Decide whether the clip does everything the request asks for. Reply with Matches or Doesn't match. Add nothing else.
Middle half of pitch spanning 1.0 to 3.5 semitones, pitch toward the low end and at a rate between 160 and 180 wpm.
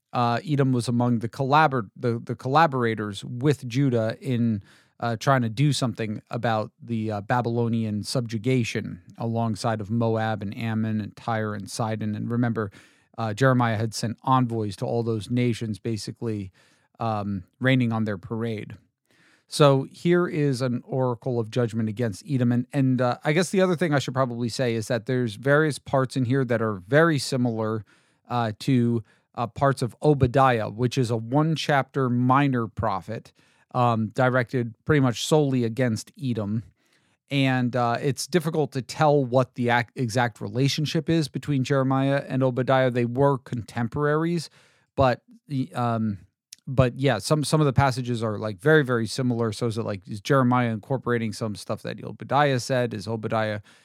Matches